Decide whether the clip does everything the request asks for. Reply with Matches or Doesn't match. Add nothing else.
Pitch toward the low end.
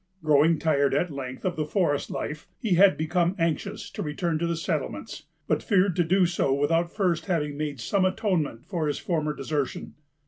Doesn't match